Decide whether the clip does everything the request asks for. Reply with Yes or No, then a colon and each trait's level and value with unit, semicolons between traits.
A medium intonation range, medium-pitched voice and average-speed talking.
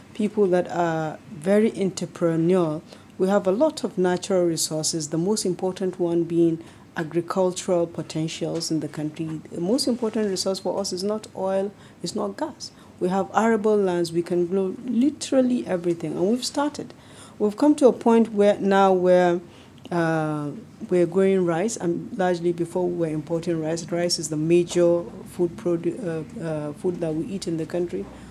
Yes: average, 3.0 semitones; medium, 180 Hz; average, 170 wpm